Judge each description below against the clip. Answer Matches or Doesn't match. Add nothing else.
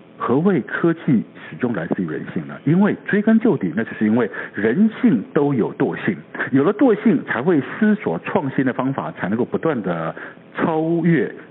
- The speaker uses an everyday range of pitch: Doesn't match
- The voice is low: Doesn't match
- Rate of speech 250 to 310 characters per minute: Matches